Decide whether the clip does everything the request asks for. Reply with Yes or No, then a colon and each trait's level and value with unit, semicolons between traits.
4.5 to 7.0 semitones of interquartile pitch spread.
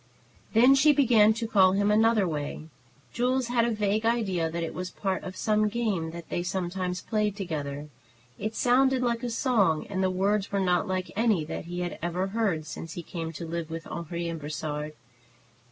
Yes: average, 4.8 semitones